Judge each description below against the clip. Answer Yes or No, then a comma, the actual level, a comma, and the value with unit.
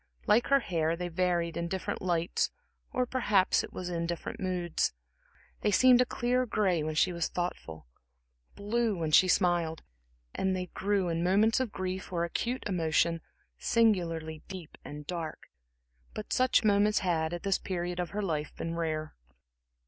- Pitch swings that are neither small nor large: Yes, average, 3.5 semitones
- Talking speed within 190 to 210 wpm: No, average, 165 wpm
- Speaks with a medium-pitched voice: Yes, medium, 180 Hz